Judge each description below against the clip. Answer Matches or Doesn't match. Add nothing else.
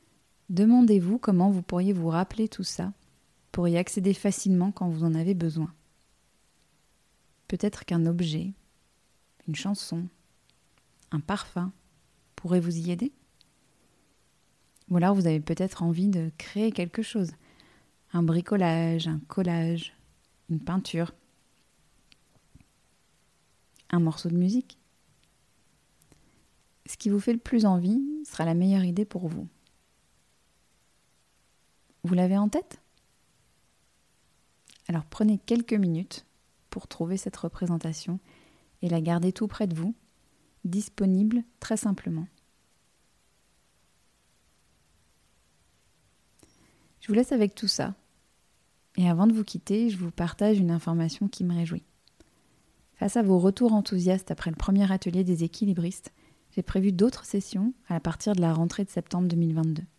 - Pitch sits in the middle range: Matches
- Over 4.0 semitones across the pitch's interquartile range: Doesn't match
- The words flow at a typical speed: Doesn't match